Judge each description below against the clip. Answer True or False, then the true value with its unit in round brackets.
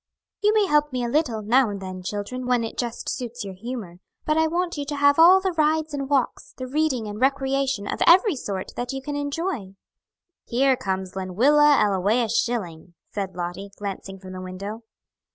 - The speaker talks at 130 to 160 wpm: False (190 wpm)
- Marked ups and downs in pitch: True (6.5 semitones)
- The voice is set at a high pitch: True (245 Hz)